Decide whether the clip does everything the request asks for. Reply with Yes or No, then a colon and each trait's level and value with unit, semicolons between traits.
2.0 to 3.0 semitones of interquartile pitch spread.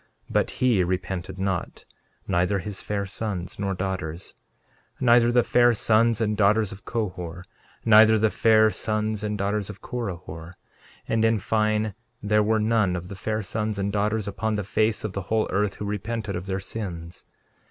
Yes: narrow, 2.5 semitones